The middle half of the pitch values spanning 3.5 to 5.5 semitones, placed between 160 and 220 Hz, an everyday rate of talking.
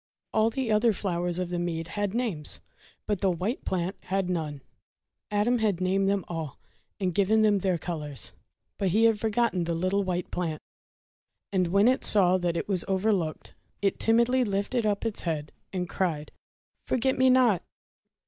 Yes: average, 3.8 semitones; high, 190 Hz; average, 175 wpm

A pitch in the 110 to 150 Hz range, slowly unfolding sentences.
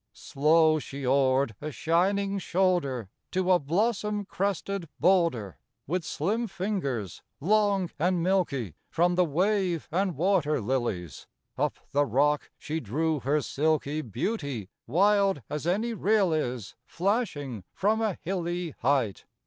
No: medium, 165 Hz; slow, 125 wpm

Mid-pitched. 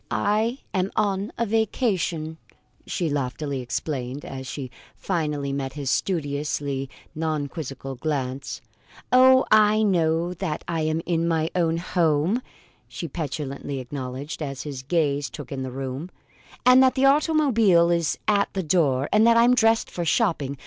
Yes: medium, 160 Hz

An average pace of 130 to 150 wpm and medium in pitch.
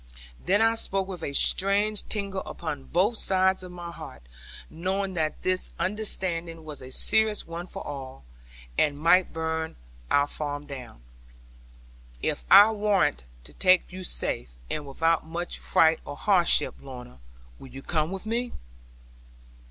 Yes: average, 145 wpm; medium, 170 Hz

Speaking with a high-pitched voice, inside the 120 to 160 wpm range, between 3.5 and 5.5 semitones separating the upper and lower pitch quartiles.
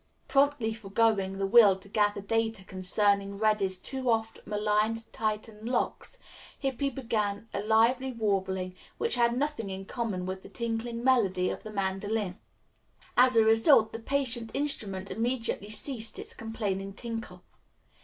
No: high, 220 Hz; average, 140 wpm; average, 3.0 semitones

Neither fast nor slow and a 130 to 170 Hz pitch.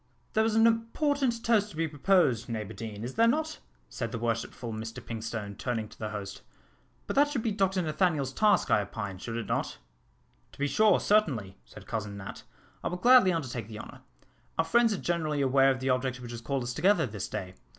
No: fast, 210 wpm; low, 135 Hz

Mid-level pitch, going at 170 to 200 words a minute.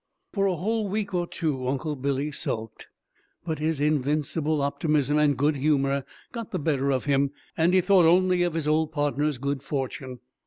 Yes: medium, 150 Hz; average, 180 wpm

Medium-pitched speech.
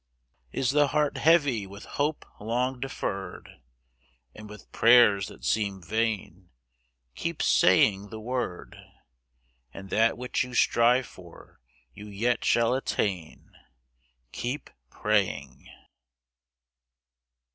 No: low, 115 Hz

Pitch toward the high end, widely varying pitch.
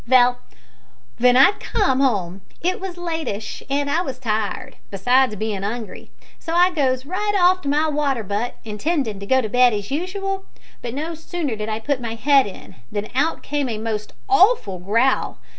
Yes: very high, 260 Hz; wide, 6.8 semitones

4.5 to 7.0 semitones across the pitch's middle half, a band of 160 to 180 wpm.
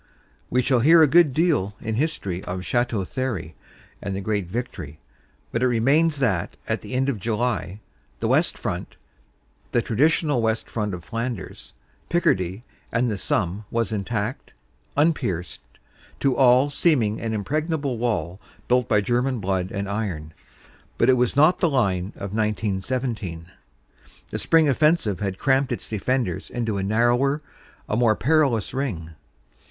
No: average, 5.1 semitones; average, 150 wpm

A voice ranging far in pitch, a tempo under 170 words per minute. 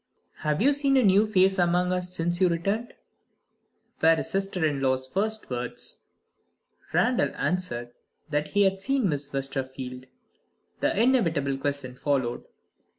Yes: wide, 6.1 semitones; average, 140 wpm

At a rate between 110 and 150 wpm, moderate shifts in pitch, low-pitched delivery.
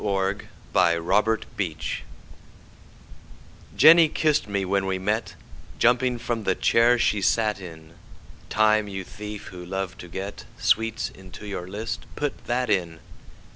Yes: slow, 135 wpm; average, 3.1 semitones; low, 100 Hz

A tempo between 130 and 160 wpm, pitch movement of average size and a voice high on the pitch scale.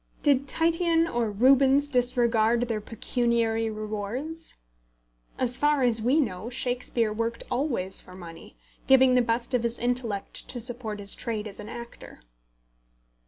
Yes: average, 140 wpm; average, 3.0 semitones; high, 235 Hz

